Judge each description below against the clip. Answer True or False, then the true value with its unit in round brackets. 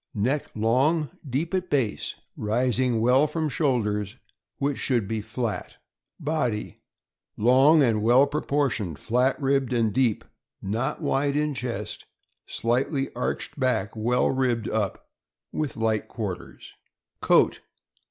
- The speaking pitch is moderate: False (125 Hz)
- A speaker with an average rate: False (125 wpm)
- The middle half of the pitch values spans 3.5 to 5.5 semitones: True (4.0 semitones)